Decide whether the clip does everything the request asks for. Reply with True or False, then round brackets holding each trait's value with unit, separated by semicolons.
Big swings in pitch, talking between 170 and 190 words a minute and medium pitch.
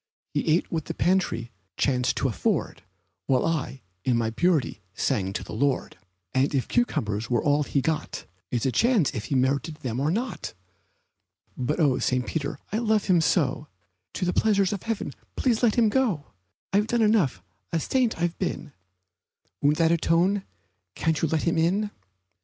True (7.0 semitones; 175 wpm; 160 Hz)